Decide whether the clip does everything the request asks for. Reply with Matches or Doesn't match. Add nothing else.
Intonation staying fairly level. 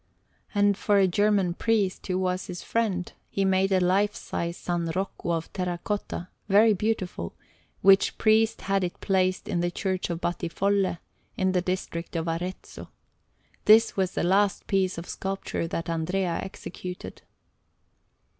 Matches